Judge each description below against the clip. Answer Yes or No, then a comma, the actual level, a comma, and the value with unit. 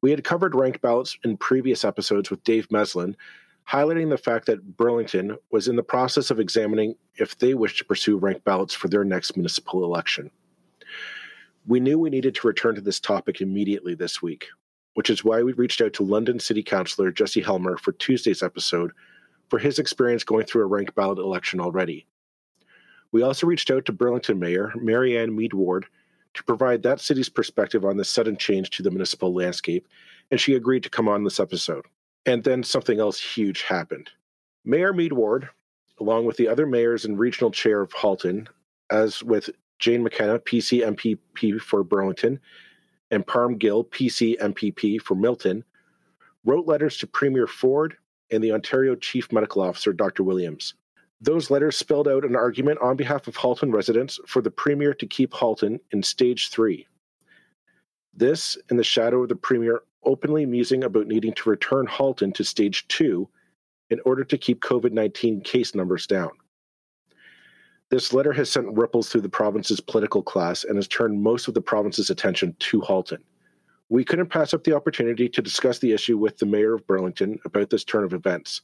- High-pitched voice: No, low, 115 Hz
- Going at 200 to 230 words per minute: No, average, 180 wpm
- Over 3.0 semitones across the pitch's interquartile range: Yes, average, 3.7 semitones